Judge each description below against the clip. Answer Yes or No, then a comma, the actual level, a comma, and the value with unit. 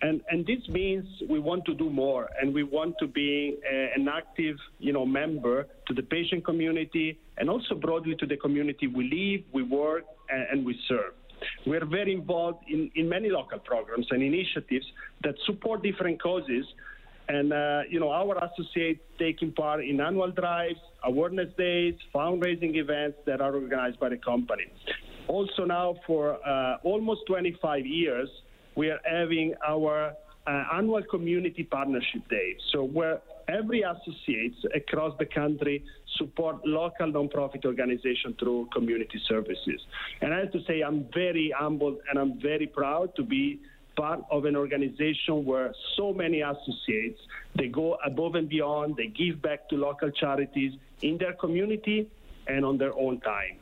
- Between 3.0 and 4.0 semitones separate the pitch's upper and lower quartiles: Yes, average, 3.7 semitones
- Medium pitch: Yes, medium, 155 Hz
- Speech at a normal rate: Yes, average, 160 wpm